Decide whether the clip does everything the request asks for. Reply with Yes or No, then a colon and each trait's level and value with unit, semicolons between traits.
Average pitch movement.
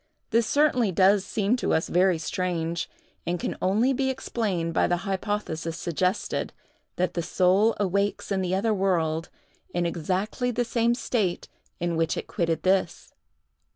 Yes: average, 3.8 semitones